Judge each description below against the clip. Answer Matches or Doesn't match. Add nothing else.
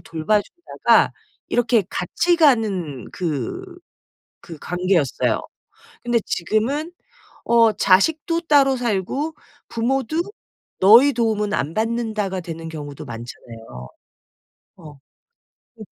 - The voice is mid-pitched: Doesn't match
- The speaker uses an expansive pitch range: Matches